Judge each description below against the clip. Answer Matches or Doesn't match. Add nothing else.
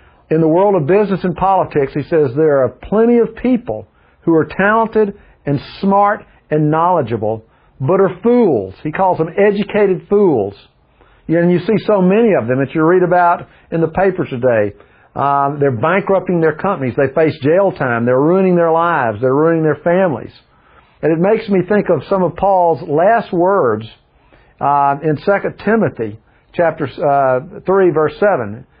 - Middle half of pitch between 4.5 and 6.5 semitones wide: Matches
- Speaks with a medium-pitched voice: Matches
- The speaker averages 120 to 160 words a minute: Doesn't match